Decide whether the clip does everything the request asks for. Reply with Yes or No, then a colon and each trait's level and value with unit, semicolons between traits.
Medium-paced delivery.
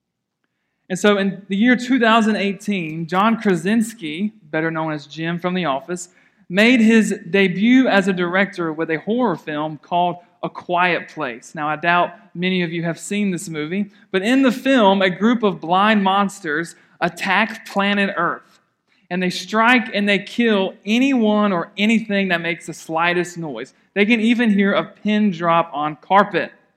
Yes: average, 165 wpm